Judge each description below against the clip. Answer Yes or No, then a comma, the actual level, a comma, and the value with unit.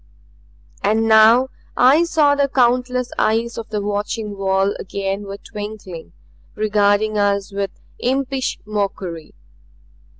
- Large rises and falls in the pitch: No, average, 3.5 semitones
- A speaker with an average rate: No, slow, 110 wpm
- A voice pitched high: Yes, high, 215 Hz